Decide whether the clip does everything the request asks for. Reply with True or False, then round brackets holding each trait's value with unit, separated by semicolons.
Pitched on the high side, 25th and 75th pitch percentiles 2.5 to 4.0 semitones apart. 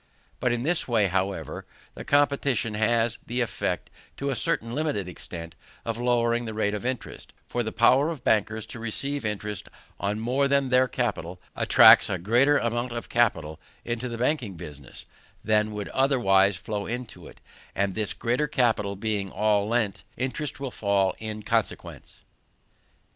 False (115 Hz; 3.5 semitones)